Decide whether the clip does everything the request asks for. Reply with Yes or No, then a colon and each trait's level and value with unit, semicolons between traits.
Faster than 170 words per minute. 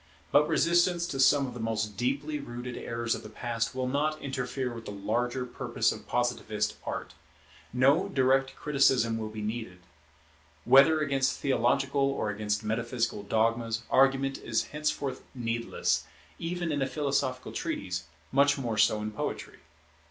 No: average, 150 wpm